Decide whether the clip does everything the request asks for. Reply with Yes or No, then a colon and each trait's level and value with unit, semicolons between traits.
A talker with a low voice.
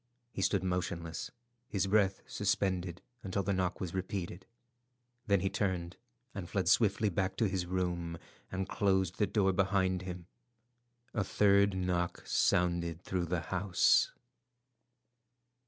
Yes: very low, 95 Hz